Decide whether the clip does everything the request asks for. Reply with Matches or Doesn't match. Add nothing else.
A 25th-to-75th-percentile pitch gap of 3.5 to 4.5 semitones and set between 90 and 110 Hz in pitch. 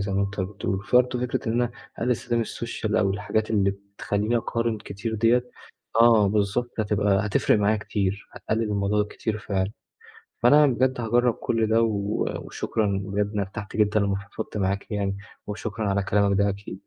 Doesn't match